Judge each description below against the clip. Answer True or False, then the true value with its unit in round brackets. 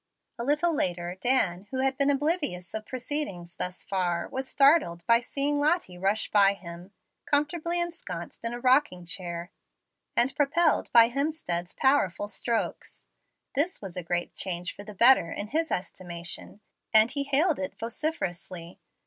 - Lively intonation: True (8.1 semitones)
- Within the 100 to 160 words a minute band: True (150 wpm)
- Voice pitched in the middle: False (230 Hz)